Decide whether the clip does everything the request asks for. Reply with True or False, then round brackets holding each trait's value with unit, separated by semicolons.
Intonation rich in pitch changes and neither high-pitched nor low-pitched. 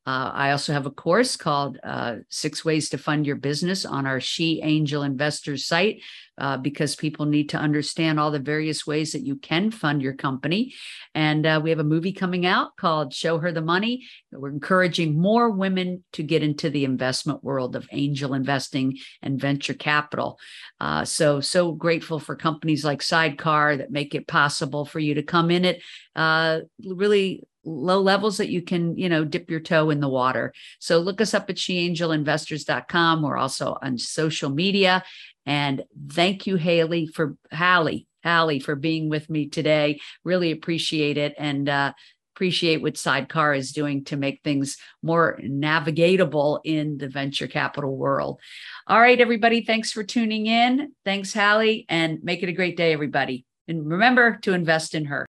False (3.4 semitones; 160 Hz)